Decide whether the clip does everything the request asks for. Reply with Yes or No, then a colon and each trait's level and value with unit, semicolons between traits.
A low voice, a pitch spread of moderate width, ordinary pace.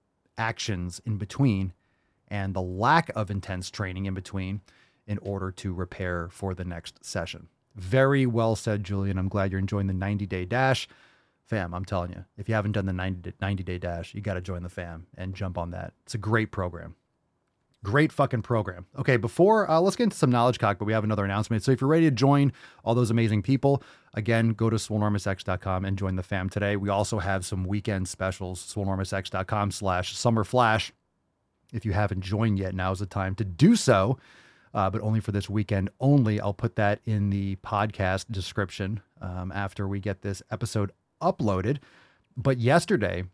Yes: low, 100 Hz; average, 3.2 semitones; average, 190 wpm